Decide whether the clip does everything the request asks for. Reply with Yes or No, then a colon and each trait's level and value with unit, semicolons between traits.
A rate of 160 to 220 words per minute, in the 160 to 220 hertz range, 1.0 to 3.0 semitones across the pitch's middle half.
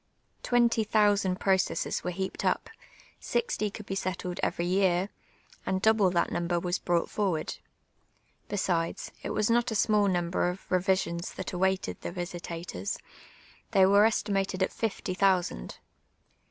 No: average, 145 wpm; high, 190 Hz; narrow, 2.6 semitones